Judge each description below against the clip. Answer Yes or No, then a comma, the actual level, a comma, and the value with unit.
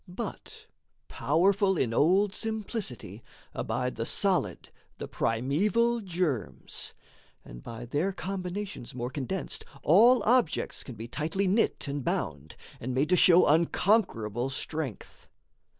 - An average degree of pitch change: No, wide, 7.8 semitones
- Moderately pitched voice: Yes, medium, 165 Hz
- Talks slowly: Yes, slow, 120 wpm